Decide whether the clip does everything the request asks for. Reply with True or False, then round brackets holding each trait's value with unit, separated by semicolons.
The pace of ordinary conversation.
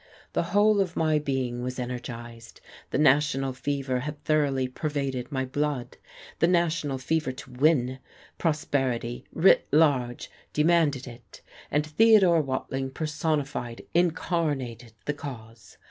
False (120 wpm)